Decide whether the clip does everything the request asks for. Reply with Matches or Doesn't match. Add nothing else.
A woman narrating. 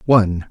Doesn't match